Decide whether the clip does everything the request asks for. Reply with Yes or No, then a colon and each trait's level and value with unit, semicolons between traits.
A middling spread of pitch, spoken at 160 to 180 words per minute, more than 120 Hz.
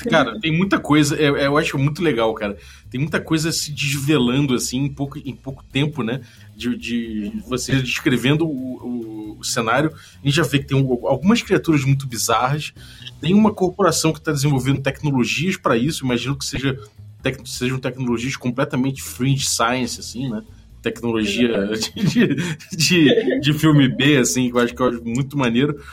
Yes: average, 3.6 semitones; average, 170 wpm; low, 135 Hz